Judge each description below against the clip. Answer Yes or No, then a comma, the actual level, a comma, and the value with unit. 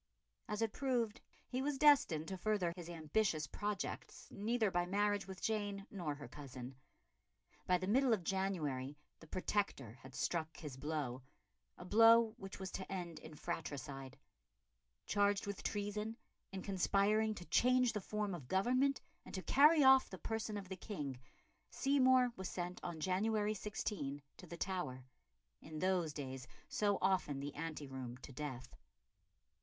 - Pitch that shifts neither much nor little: No, wide, 5.7 semitones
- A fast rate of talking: No, average, 155 wpm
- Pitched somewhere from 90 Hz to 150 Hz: No, high, 190 Hz